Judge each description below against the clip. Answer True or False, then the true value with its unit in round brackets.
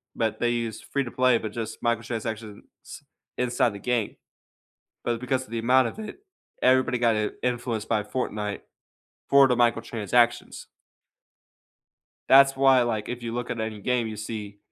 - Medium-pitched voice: False (120 Hz)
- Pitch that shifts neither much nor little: False (2.1 semitones)